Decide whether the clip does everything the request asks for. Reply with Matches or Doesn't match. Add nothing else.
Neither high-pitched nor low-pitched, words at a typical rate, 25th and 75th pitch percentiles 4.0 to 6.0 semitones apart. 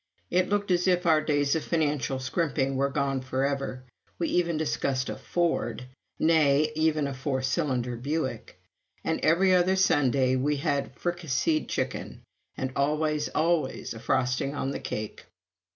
Doesn't match